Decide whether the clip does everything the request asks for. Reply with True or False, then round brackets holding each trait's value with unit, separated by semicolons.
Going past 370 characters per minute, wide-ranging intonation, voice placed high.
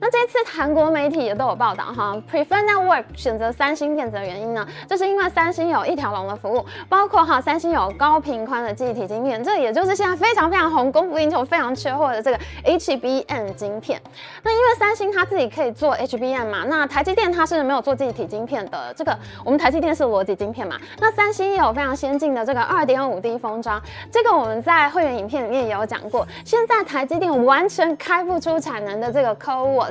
True (380 characters per minute; 6.2 semitones; 295 Hz)